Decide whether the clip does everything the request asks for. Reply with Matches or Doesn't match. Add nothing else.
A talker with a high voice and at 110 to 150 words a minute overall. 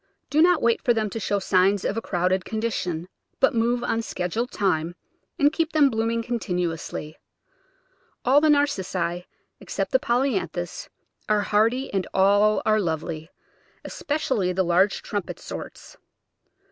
Matches